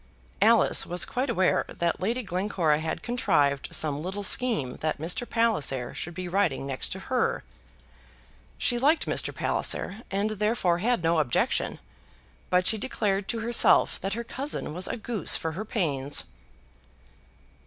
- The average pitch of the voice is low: No, high, 190 Hz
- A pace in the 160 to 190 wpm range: No, average, 150 wpm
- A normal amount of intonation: No, wide, 6.2 semitones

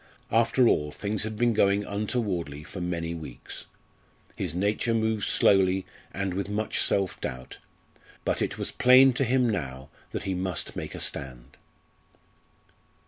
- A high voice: No, low, 100 Hz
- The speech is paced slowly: No, average, 145 wpm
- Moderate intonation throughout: Yes, average, 4.7 semitones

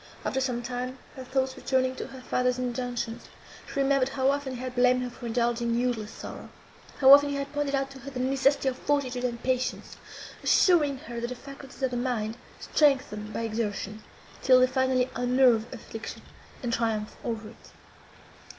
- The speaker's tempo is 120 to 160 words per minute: No, average, 180 wpm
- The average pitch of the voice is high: Yes, very high, 255 Hz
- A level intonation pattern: Yes, narrow, 1.9 semitones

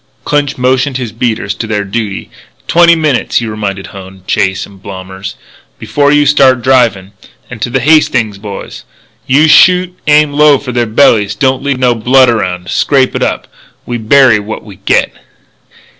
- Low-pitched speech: Yes, low, 120 Hz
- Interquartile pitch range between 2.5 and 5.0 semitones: No, wide, 5.4 semitones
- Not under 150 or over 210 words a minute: Yes, average, 170 wpm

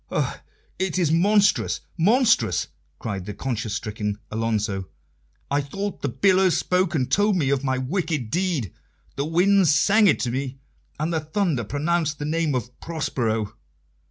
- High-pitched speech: No, medium, 150 Hz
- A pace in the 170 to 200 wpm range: No, average, 155 wpm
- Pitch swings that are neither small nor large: No, wide, 7.0 semitones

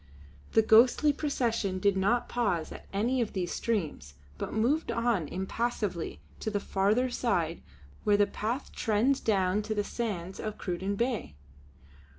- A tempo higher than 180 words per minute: No, average, 150 wpm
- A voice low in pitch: No, high, 215 Hz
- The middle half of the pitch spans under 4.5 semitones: Yes, average, 3.8 semitones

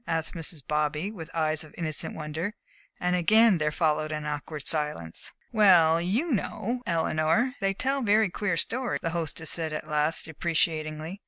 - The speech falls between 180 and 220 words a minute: No, average, 160 wpm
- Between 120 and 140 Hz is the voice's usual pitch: No, medium, 165 Hz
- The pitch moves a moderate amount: Yes, average, 4.1 semitones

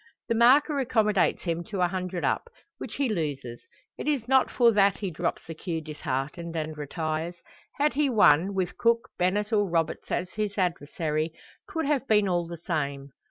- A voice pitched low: No, medium, 180 Hz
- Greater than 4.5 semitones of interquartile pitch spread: Yes, wide, 5.6 semitones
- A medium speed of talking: Yes, average, 180 wpm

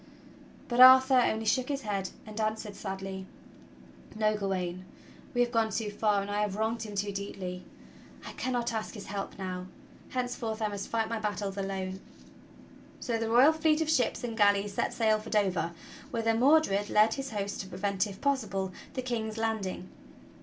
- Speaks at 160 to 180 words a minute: Yes, average, 175 wpm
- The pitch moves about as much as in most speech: Yes, average, 3.0 semitones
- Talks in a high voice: Yes, high, 215 Hz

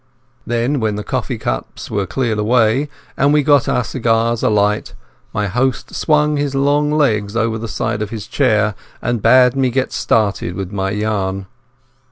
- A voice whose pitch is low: Yes, low, 115 Hz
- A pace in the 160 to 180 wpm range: Yes, average, 175 wpm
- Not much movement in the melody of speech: No, average, 4.2 semitones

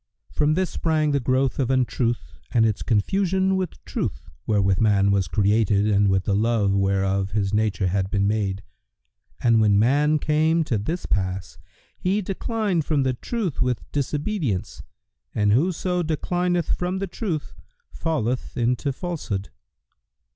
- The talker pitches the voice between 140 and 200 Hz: No, low, 120 Hz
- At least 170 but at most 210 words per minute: No, average, 145 wpm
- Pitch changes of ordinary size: No, wide, 8.3 semitones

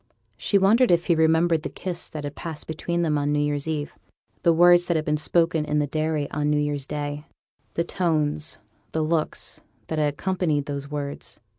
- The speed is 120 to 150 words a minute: No, average, 195 wpm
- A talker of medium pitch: Yes, medium, 155 Hz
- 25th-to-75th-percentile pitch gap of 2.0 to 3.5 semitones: Yes, narrow, 2.4 semitones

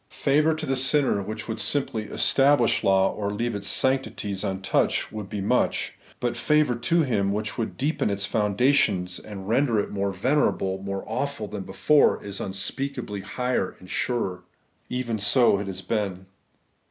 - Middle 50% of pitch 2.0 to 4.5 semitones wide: No, average, 5.1 semitones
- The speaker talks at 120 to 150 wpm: No, average, 160 wpm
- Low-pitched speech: Yes, low, 110 Hz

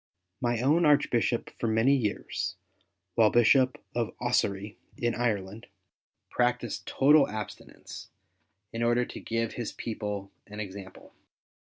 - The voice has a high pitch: No, low, 115 Hz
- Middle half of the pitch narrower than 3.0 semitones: Yes, narrow, 2.6 semitones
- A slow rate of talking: Yes, slow, 115 wpm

